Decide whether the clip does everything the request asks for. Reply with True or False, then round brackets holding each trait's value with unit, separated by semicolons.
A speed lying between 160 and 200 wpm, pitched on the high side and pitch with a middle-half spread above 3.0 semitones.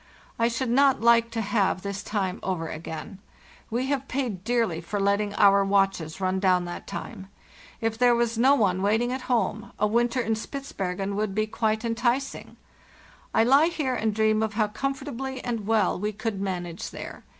True (180 wpm; 220 Hz; 3.4 semitones)